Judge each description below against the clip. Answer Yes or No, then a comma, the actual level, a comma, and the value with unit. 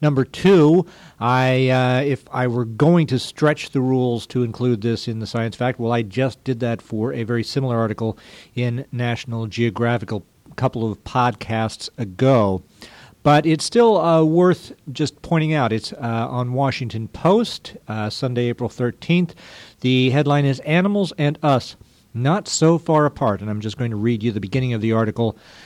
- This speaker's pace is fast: No, average, 180 wpm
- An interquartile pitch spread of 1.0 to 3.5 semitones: No, average, 4.1 semitones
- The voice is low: Yes, low, 125 Hz